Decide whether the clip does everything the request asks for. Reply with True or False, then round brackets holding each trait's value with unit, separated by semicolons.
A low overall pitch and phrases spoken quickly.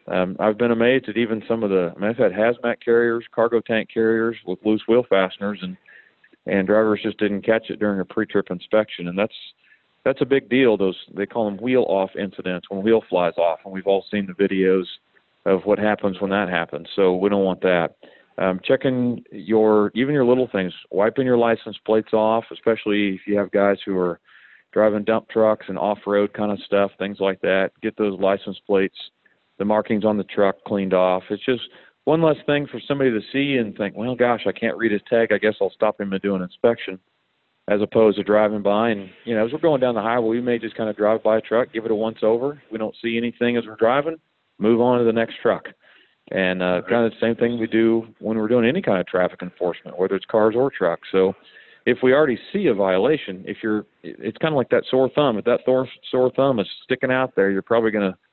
True (110 Hz; 235 wpm)